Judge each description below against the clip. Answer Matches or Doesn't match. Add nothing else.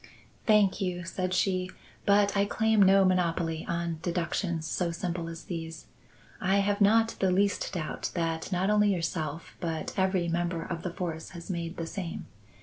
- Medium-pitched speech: Matches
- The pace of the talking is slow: Doesn't match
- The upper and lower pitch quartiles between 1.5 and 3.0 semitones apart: Matches